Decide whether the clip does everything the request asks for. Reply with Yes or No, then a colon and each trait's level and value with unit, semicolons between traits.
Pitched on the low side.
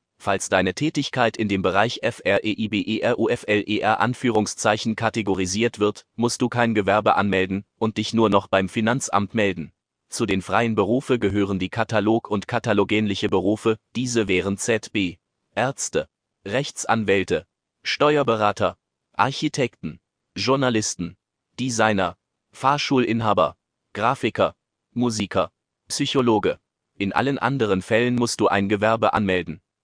Yes: low, 110 Hz